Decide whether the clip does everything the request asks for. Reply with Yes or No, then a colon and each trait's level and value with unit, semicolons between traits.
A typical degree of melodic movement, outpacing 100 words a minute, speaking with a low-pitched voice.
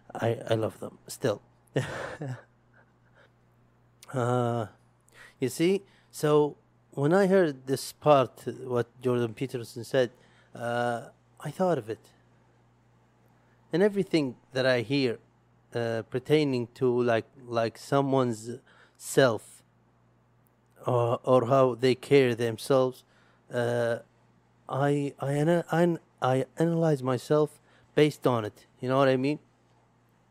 Yes: average, 3.4 semitones; average, 110 wpm; low, 130 Hz